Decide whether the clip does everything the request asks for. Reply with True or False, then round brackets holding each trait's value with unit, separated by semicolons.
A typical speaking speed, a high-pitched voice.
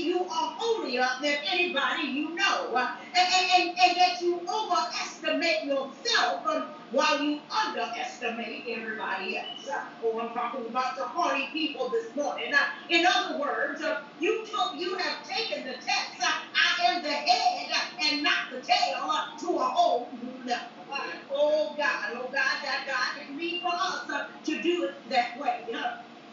True (165 wpm; 305 Hz)